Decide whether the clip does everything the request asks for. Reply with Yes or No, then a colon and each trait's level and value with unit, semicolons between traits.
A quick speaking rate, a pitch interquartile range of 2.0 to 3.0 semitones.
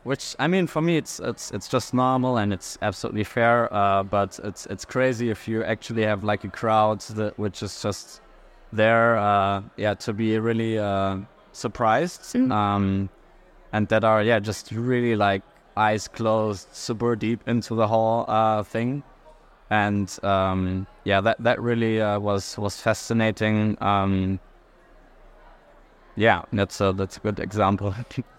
No: average, 155 wpm; narrow, 2.5 semitones